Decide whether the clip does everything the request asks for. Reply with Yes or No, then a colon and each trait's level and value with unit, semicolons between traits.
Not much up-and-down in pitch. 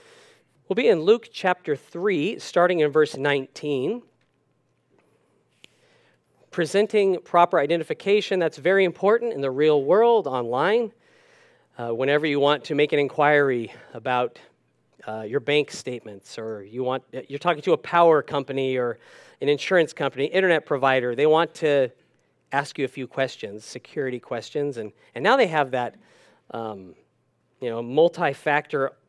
No: average, 4.9 semitones